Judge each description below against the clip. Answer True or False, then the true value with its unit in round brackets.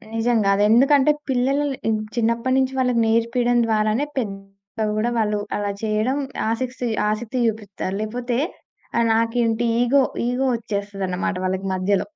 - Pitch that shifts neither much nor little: True (3.1 semitones)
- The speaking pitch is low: False (230 Hz)